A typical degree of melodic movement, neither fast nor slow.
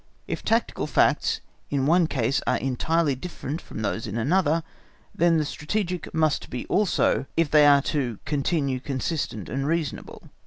Yes: average, 3.9 semitones; average, 160 wpm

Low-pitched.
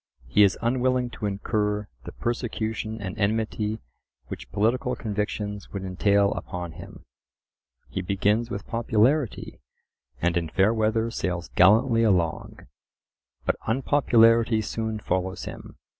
Yes: low, 105 Hz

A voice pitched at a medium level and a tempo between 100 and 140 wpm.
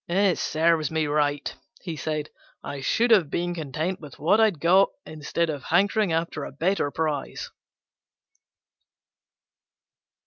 Yes: medium, 160 Hz; slow, 135 wpm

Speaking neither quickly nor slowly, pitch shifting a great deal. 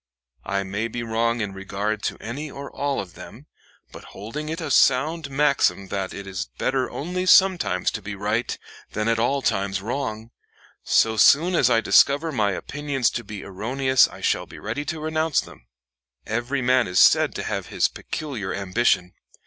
Yes: average, 180 wpm; wide, 5.9 semitones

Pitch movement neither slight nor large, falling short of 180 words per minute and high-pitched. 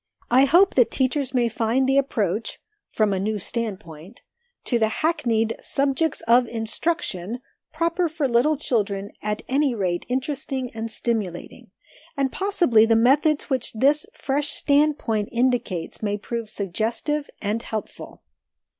Yes: average, 4.5 semitones; slow, 135 wpm; high, 240 Hz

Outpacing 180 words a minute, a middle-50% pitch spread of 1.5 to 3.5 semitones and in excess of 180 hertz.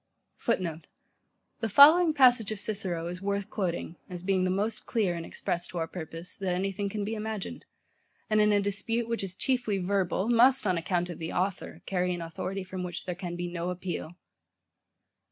Yes: average, 190 wpm; average, 3.2 semitones; high, 190 Hz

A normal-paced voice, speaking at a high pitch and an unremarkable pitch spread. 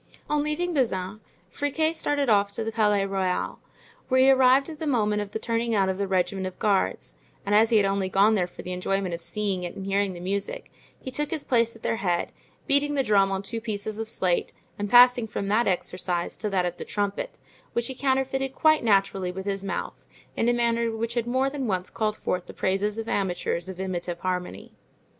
No: fast, 220 wpm; high, 210 Hz; average, 4.3 semitones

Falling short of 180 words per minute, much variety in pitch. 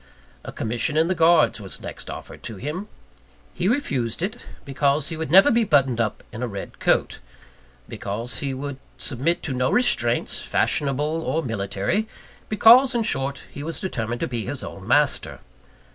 Yes: average, 170 wpm; wide, 6.1 semitones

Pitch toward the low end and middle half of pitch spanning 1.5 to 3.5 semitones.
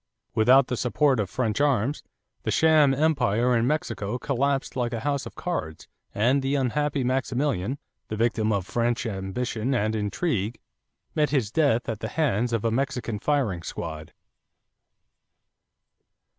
No: low, 125 Hz; average, 4.3 semitones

